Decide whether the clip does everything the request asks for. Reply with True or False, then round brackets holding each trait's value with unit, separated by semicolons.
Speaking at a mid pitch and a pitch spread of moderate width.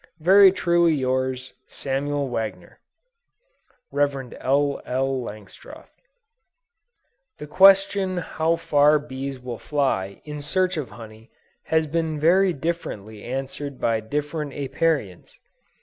True (145 Hz; 4.0 semitones)